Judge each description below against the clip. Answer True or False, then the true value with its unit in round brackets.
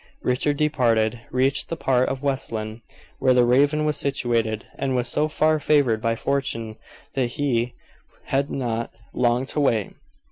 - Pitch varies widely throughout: False (3.3 semitones)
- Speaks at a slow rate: False (155 wpm)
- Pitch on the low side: True (130 Hz)